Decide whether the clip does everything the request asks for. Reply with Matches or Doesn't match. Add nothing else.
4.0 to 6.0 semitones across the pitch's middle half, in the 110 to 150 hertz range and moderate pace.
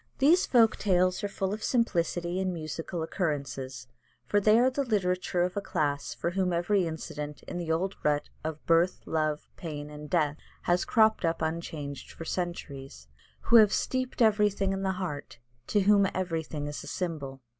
Doesn't match